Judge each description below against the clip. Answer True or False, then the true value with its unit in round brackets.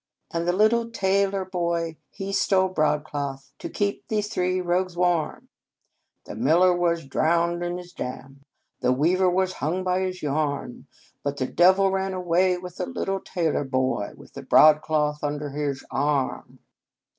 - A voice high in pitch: False (175 Hz)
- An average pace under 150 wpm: False (160 wpm)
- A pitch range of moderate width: True (4.0 semitones)